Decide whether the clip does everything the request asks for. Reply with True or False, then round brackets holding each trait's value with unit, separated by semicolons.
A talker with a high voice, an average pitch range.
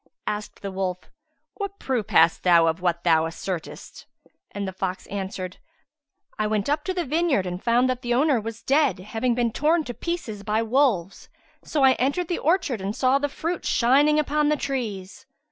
False (235 Hz; 7.0 semitones)